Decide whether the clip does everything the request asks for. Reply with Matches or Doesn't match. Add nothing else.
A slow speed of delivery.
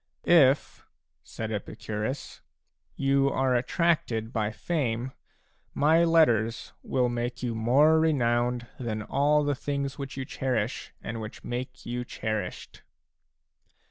Matches